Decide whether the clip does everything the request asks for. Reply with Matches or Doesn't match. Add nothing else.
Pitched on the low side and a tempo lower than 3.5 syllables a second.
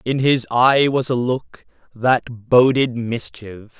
Matches